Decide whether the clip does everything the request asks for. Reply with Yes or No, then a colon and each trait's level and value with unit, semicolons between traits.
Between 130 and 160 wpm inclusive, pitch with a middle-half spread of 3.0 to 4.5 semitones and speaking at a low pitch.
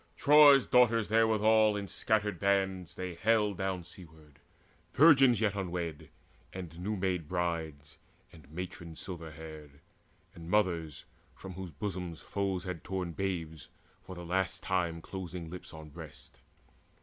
Yes: slow, 135 wpm; average, 3.3 semitones; very low, 90 Hz